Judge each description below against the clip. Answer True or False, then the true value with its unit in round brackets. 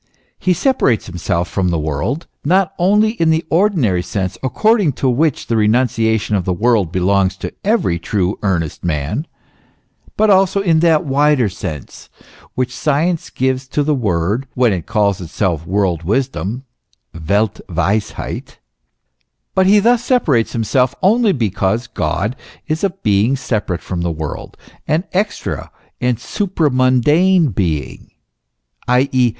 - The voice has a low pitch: True (125 Hz)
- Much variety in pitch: True (9.0 semitones)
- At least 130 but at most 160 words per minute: True (140 wpm)